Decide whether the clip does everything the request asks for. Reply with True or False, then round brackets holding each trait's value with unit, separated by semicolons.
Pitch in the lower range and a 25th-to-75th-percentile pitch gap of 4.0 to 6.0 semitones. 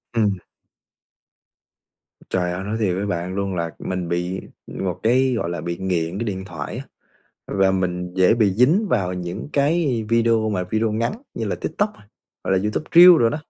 True (100 Hz; 4.3 semitones)